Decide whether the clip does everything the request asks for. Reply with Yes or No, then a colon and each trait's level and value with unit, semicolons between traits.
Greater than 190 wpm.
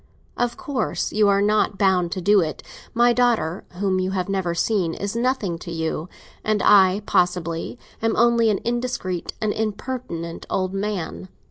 No: average, 160 wpm